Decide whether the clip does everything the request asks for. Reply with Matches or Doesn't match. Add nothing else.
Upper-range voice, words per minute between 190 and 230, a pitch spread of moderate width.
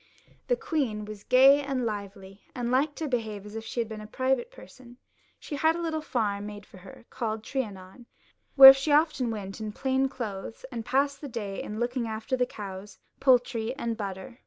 Matches